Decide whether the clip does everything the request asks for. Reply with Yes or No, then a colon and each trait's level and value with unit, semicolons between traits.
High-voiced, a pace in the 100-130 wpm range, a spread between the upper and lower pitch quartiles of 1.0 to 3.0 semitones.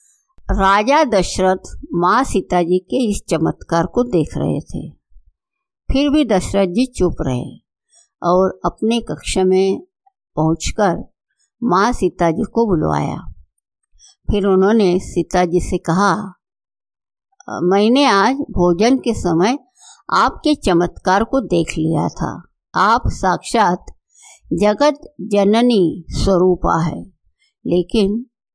No: high, 195 Hz; slow, 110 wpm; average, 5.3 semitones